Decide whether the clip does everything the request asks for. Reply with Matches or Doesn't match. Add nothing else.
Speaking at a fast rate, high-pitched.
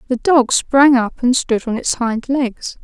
Matches